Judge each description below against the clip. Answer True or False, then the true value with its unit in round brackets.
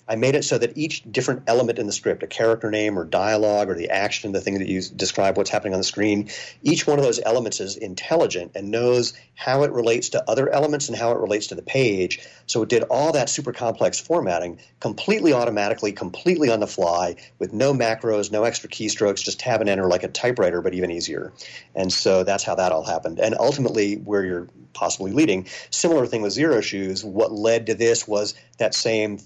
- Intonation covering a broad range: False (3.4 semitones)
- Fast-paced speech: True (215 wpm)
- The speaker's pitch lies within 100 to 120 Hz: True (105 Hz)